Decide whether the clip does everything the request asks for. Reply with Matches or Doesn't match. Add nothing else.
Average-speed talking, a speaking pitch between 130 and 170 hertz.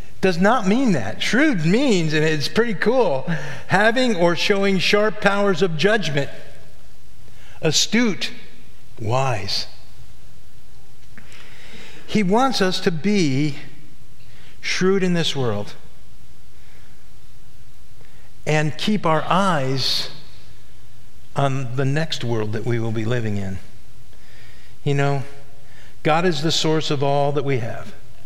Doesn't match